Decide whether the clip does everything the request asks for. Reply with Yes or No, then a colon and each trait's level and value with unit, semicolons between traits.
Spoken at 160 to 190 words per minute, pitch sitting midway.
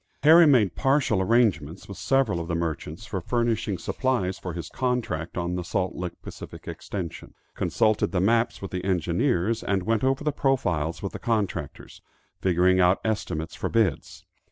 No: average, 165 wpm; very low, 95 Hz